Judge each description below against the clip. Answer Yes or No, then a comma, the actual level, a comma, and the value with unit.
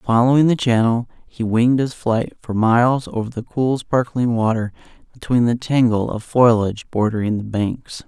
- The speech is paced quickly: No, average, 165 wpm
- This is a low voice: Yes, low, 115 Hz